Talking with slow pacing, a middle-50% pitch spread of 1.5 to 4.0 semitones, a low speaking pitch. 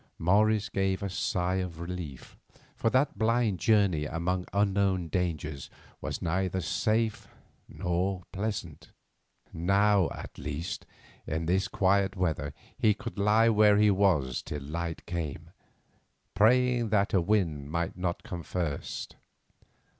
Yes: slow, 125 wpm; average, 3.5 semitones; very low, 95 Hz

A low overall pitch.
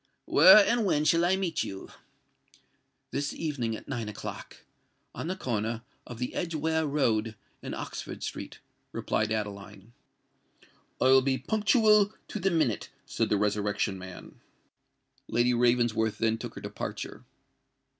Yes: low, 125 Hz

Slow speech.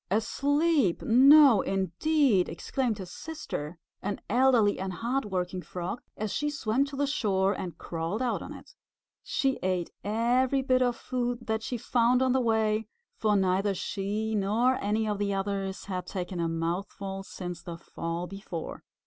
No: average, 160 wpm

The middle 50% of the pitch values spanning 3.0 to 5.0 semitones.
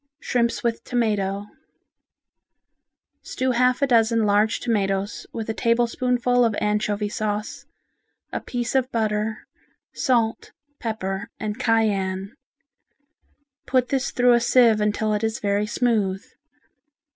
No: narrow, 2.5 semitones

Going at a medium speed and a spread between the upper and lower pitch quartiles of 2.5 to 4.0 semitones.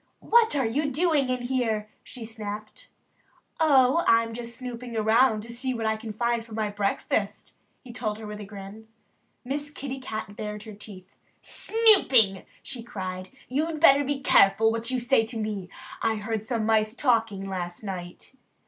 Yes: average, 180 wpm; average, 3.5 semitones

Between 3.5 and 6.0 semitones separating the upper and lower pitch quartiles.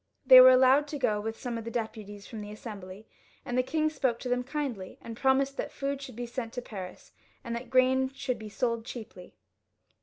No: average, 3.1 semitones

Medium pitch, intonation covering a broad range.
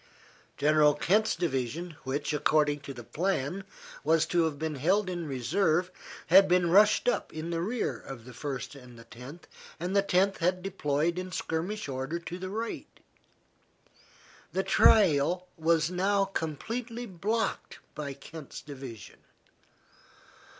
No: medium, 165 Hz; average, 4.6 semitones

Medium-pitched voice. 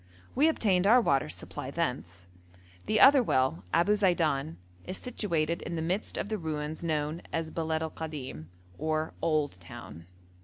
Yes: medium, 160 Hz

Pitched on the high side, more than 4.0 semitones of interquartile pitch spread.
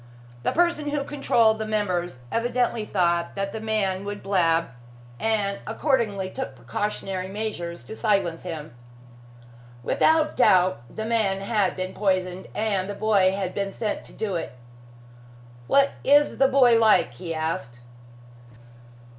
No: high, 200 Hz; average, 3.4 semitones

